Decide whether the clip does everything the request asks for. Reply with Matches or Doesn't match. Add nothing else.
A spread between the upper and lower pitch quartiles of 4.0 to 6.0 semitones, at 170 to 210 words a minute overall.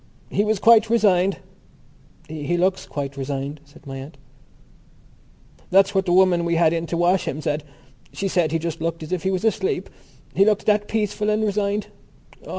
Matches